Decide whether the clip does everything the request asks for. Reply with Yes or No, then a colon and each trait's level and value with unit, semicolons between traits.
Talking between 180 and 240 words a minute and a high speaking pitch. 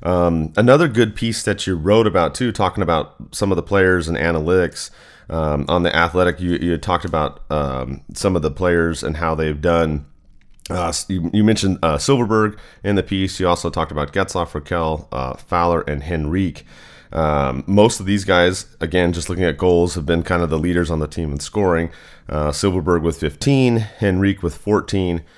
No: average, 195 wpm; very low, 85 Hz